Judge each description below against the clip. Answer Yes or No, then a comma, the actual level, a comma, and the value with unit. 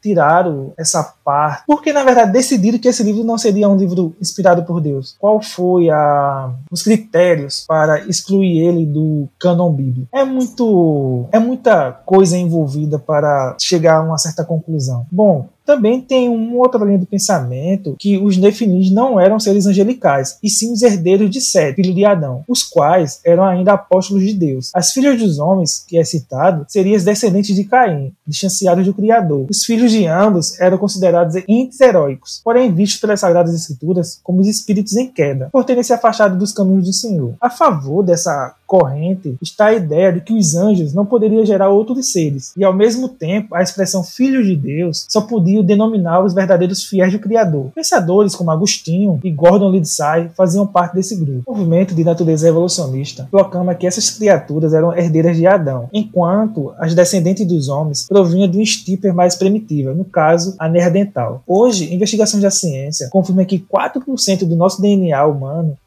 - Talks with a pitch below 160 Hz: No, medium, 185 Hz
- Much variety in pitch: No, average, 4.1 semitones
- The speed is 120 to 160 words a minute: No, average, 175 wpm